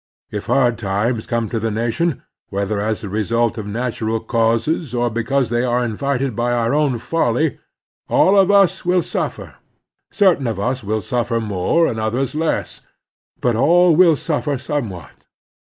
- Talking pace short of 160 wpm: No, average, 165 wpm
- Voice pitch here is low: Yes, low, 120 Hz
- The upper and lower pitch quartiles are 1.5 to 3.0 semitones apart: No, average, 4.8 semitones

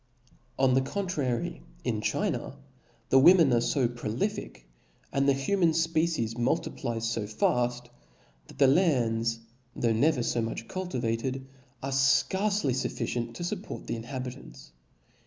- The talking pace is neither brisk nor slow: No, slow, 125 wpm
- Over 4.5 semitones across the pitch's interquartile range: Yes, wide, 5.4 semitones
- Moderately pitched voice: No, low, 130 Hz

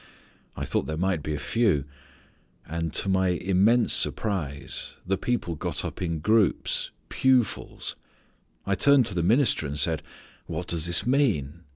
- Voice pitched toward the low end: Yes, very low, 90 Hz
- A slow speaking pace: No, average, 160 wpm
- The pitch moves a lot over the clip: Yes, wide, 5.7 semitones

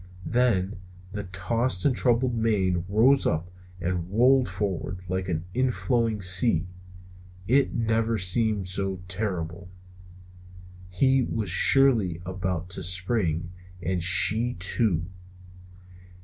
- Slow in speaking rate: Yes, slow, 105 wpm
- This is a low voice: Yes, very low, 95 Hz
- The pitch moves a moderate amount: Yes, average, 4.3 semitones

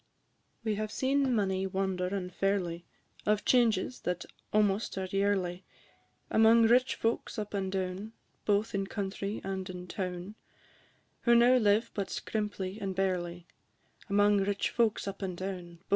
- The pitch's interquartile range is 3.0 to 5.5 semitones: No, narrow, 2.4 semitones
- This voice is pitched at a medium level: No, high, 195 Hz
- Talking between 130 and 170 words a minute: Yes, average, 145 wpm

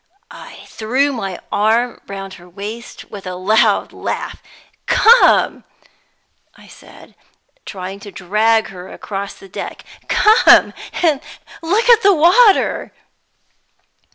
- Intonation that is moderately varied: No, wide, 7.8 semitones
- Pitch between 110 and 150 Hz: No, high, 220 Hz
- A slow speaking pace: Yes, slow, 115 wpm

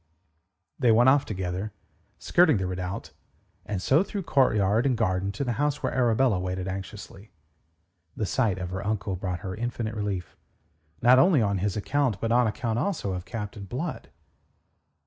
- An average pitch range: Yes, average, 4.7 semitones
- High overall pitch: No, low, 105 Hz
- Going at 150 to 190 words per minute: Yes, average, 165 wpm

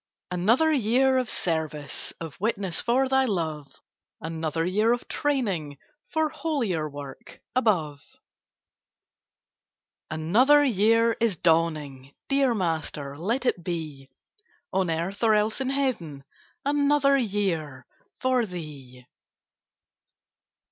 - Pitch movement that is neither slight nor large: No, wide, 8.4 semitones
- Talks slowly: Yes, slow, 105 wpm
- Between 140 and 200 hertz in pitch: Yes, high, 190 Hz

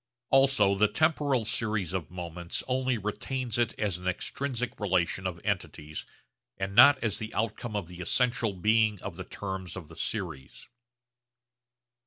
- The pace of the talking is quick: No, average, 150 wpm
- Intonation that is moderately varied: Yes, average, 4.8 semitones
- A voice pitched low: Yes, low, 105 Hz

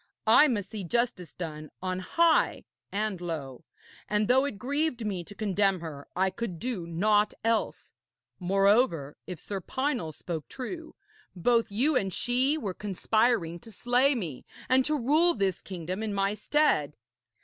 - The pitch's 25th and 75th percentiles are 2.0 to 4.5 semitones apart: No, wide, 5.5 semitones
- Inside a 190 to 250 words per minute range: No, average, 155 wpm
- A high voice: Yes, high, 205 Hz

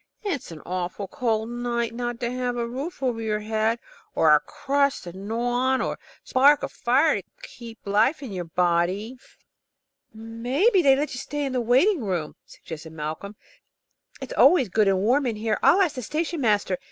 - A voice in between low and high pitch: No, high, 235 Hz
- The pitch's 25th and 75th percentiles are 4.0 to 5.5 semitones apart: Yes, average, 4.4 semitones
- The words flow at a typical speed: Yes, average, 190 wpm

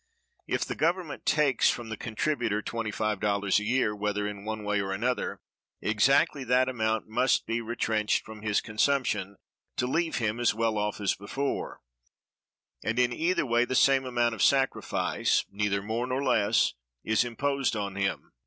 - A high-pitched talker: No, low, 115 Hz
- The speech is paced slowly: No, average, 160 wpm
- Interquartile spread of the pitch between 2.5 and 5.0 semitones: Yes, average, 3.5 semitones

